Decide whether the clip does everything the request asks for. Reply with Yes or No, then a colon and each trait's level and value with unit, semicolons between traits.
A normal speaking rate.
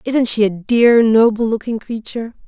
Yes: average, 170 wpm